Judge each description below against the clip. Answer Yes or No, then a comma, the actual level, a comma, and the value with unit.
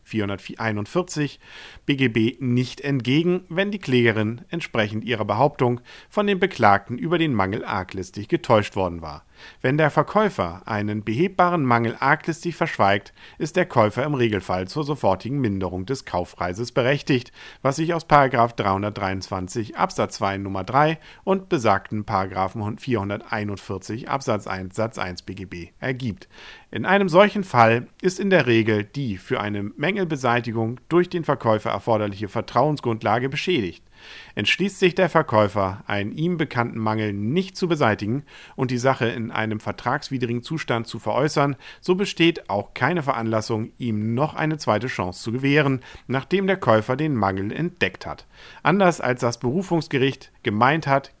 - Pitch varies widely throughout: Yes, wide, 6.5 semitones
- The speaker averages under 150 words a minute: Yes, average, 140 wpm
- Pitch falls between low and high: No, low, 120 Hz